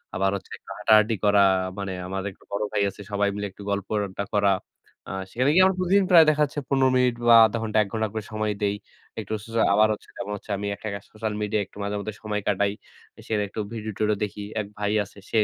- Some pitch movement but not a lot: No, narrow, 1.7 semitones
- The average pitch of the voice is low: Yes, low, 105 Hz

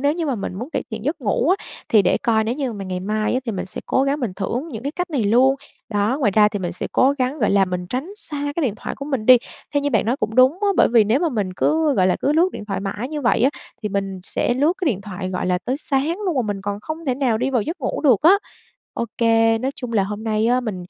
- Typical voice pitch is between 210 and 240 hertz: Yes, high, 235 Hz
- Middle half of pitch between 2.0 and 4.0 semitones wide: No, average, 5.3 semitones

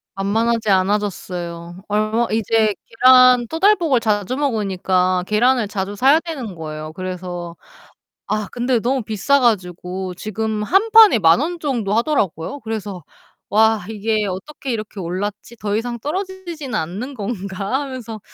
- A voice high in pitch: Yes, high, 215 Hz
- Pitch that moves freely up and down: No, average, 4.9 semitones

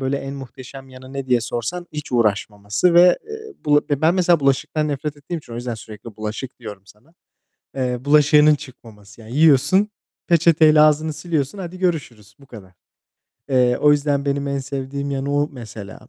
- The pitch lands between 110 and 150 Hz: Yes, medium, 140 Hz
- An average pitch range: Yes, average, 3.9 semitones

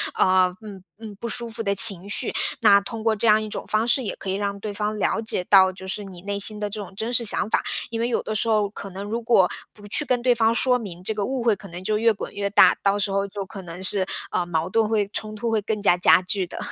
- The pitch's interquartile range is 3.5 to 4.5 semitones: No, narrow, 2.5 semitones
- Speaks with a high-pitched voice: Yes, high, 205 Hz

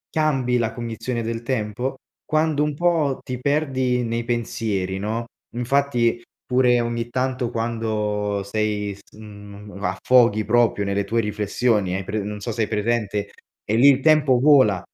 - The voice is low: Yes, low, 115 Hz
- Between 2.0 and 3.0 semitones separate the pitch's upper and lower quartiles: No, average, 3.4 semitones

